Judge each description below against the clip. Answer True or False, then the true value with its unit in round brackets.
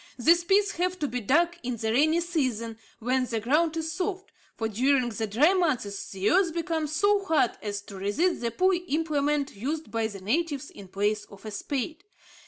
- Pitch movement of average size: False (7.1 semitones)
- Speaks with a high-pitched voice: True (280 Hz)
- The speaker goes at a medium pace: True (190 wpm)